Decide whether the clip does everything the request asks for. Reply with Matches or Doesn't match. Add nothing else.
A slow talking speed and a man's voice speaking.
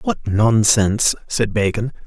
Matches